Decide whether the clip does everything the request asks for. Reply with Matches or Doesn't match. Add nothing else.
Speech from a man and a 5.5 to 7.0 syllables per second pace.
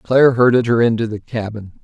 Matches